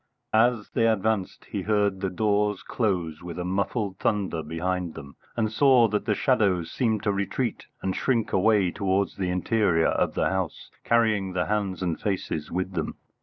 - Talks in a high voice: No, low, 100 Hz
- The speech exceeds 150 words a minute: Yes, average, 170 wpm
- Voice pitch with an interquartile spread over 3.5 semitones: No, average, 3.1 semitones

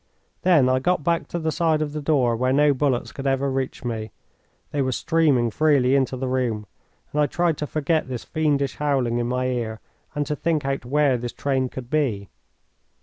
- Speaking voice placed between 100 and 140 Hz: Yes, low, 135 Hz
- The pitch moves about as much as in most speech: Yes, average, 3.0 semitones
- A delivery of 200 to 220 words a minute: Yes, fast, 205 wpm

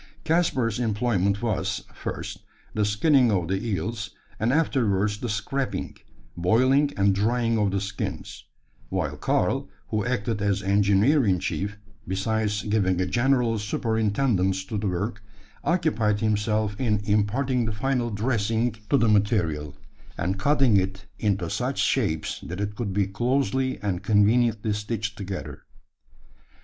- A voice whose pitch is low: Yes, low, 105 Hz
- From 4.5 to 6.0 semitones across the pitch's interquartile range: No, average, 3.1 semitones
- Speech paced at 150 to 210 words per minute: No, slow, 135 wpm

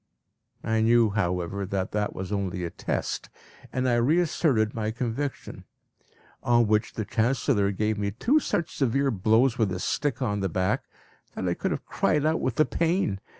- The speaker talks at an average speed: Yes, average, 175 wpm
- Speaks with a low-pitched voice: Yes, low, 110 Hz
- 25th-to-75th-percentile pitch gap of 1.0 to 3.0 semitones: No, average, 4.8 semitones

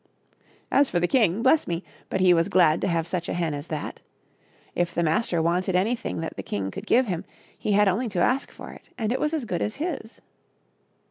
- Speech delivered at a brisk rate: Yes, fast, 225 wpm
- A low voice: No, medium, 185 Hz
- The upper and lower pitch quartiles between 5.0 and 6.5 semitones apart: Yes, average, 5.3 semitones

